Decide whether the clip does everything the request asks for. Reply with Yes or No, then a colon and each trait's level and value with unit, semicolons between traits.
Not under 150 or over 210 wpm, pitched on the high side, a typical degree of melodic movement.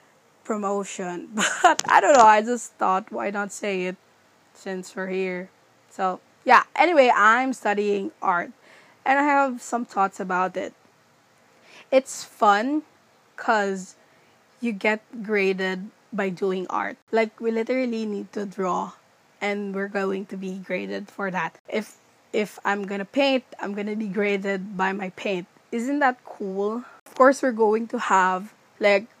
Yes: fast, 155 wpm; high, 205 Hz; average, 3.2 semitones